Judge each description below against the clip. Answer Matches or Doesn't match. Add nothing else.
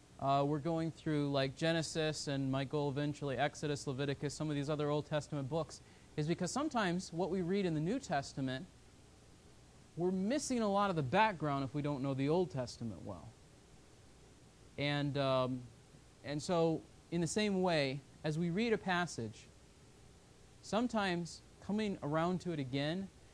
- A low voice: Doesn't match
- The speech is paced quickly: Doesn't match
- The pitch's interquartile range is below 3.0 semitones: Doesn't match